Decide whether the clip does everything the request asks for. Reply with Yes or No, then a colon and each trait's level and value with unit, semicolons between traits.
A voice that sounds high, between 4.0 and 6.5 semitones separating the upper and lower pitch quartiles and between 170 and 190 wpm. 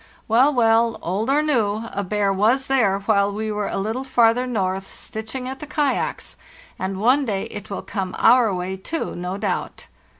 Yes: high, 220 Hz; average, 4.3 semitones; average, 180 wpm